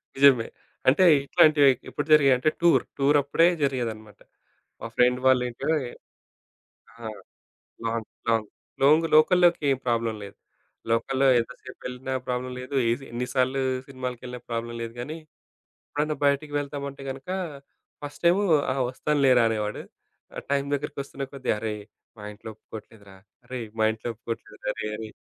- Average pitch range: Yes, average, 3.4 semitones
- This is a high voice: No, low, 130 Hz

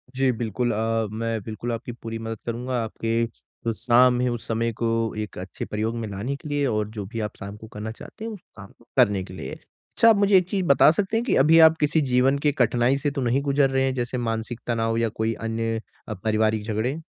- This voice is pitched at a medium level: No, low, 115 Hz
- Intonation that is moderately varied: Yes, average, 3.2 semitones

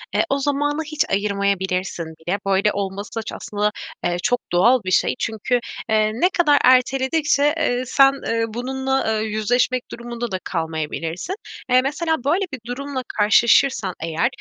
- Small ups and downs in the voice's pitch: No, average, 5.3 semitones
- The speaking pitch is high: Yes, high, 235 Hz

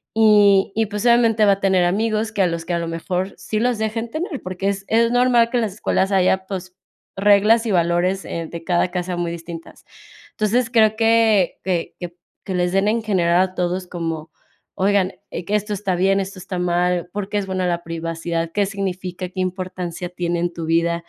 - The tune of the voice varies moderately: Yes, average, 3.2 semitones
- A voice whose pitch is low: No, high, 190 Hz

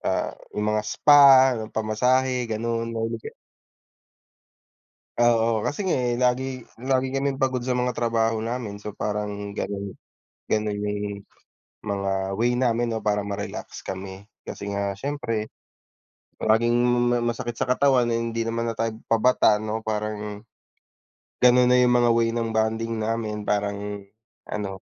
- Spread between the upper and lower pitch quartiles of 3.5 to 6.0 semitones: No, average, 2.7 semitones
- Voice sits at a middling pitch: No, low, 115 Hz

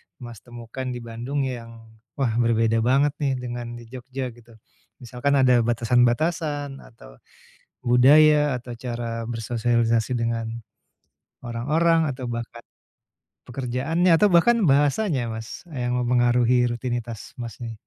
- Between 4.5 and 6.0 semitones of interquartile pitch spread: No, narrow, 2.6 semitones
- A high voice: No, low, 120 Hz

